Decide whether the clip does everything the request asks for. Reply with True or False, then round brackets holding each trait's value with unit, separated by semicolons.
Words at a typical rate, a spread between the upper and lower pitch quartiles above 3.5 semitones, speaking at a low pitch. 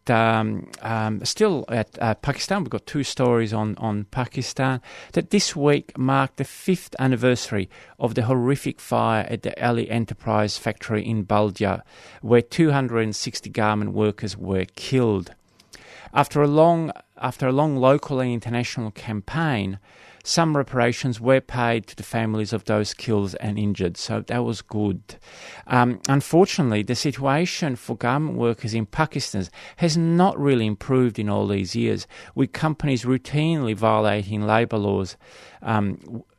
True (150 wpm; 4.2 semitones; 120 Hz)